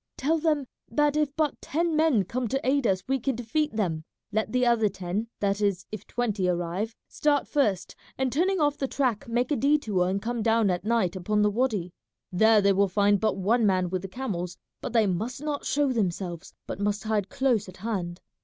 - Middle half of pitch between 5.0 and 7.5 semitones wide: Yes, wide, 5.6 semitones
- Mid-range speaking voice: No, high, 220 Hz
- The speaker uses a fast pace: Yes, fast, 210 wpm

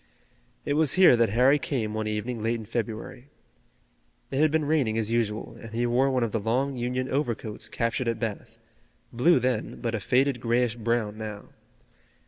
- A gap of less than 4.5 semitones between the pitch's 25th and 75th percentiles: Yes, narrow, 2.6 semitones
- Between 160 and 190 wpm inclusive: Yes, average, 180 wpm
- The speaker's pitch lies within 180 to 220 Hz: No, low, 120 Hz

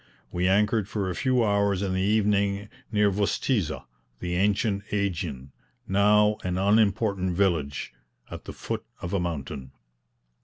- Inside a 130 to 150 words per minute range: Yes, average, 140 wpm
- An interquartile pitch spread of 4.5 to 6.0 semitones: No, narrow, 2.5 semitones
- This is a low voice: Yes, low, 100 Hz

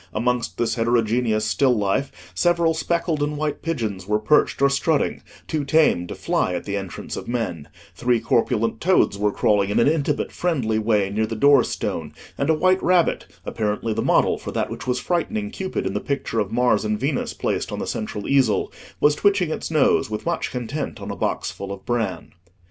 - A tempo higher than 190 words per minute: Yes, average, 200 wpm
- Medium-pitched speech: No, low, 125 Hz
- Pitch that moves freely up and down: Yes, wide, 6.1 semitones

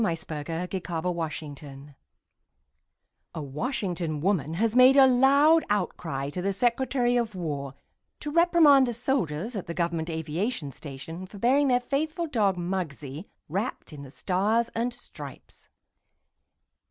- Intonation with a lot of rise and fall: Yes, wide, 7.6 semitones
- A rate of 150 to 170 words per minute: No, average, 140 wpm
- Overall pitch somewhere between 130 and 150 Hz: No, medium, 185 Hz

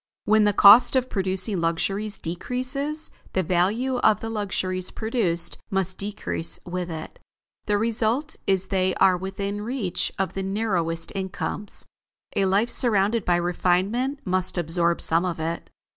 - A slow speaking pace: No, average, 145 wpm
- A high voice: Yes, high, 195 Hz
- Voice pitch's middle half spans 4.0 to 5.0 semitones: No, average, 3.5 semitones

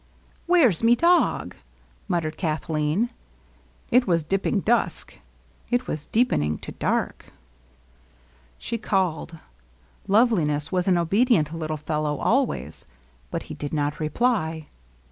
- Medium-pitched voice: Yes, medium, 170 Hz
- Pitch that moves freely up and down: Yes, wide, 7.1 semitones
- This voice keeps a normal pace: No, slow, 125 wpm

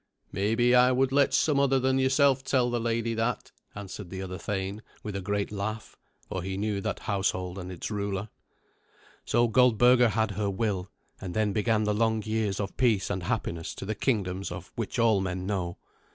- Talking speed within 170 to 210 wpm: Yes, average, 190 wpm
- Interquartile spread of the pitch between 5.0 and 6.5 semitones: No, average, 3.6 semitones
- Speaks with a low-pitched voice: Yes, low, 105 Hz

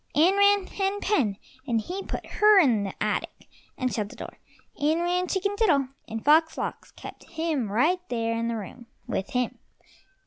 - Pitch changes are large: Yes, wide, 8.5 semitones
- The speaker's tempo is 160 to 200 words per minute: Yes, average, 180 wpm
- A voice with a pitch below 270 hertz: No, very high, 300 Hz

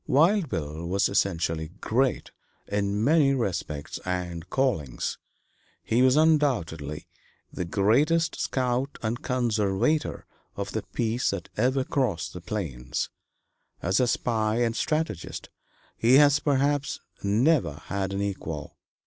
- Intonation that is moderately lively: No, wide, 6.8 semitones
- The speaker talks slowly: Yes, slow, 120 wpm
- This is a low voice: Yes, low, 110 Hz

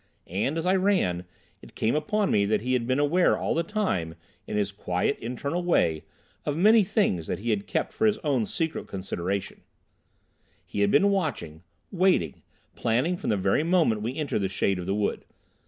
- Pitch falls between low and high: No, low, 125 Hz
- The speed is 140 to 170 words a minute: No, average, 190 wpm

